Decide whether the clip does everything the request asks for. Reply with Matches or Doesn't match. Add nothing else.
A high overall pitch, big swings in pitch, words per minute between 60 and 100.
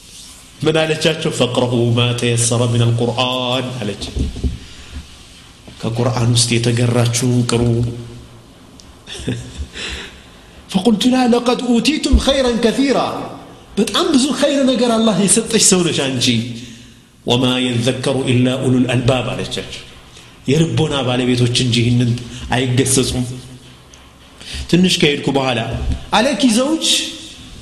Doesn't match